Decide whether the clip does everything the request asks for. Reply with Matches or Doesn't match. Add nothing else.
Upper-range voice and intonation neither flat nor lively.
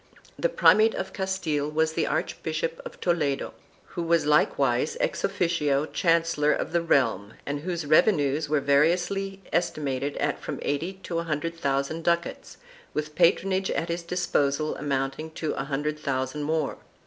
Doesn't match